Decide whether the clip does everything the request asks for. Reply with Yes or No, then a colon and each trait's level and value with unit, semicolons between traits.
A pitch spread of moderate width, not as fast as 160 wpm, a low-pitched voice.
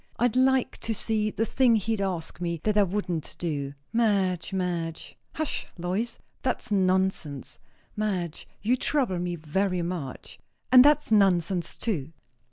No: average, 4.4 semitones; average, 140 wpm; high, 190 Hz